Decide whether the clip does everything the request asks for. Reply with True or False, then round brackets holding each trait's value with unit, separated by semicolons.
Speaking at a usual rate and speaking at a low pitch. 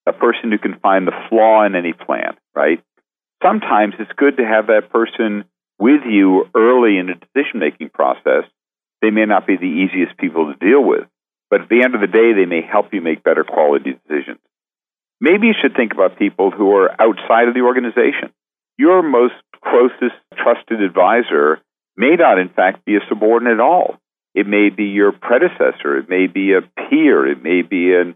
True (190 wpm; 110 Hz)